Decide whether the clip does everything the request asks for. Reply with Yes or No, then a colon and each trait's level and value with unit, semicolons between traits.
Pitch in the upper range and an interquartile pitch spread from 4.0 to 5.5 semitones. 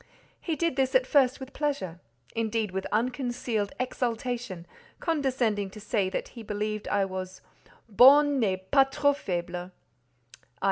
Yes: high, 230 Hz; average, 5.2 semitones